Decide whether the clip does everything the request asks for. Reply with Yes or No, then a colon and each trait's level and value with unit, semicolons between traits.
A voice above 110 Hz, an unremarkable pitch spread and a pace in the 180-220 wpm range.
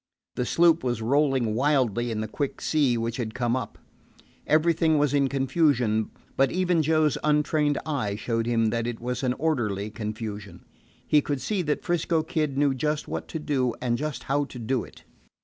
Yes: low, 135 Hz; average, 4.5 semitones; average, 185 wpm